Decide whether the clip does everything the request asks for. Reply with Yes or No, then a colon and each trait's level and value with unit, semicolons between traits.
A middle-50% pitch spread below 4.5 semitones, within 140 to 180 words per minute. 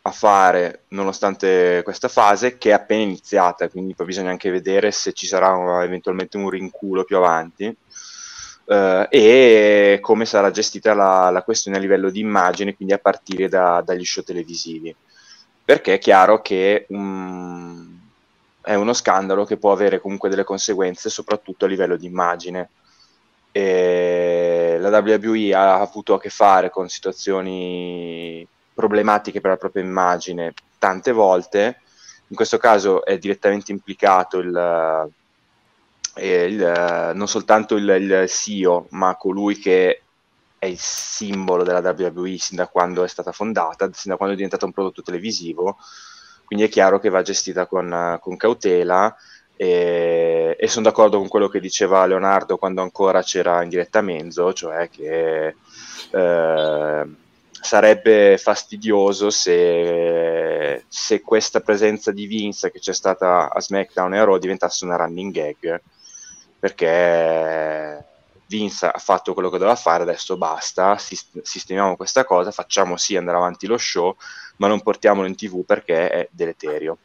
Yes: average, 2.8 semitones; average, 145 wpm